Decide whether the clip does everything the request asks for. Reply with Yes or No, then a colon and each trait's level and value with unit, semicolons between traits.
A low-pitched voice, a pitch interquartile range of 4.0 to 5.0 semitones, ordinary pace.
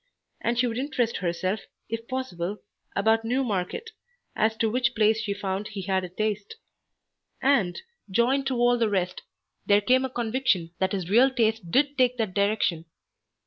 No: high, 220 Hz; average, 4.3 semitones; average, 165 wpm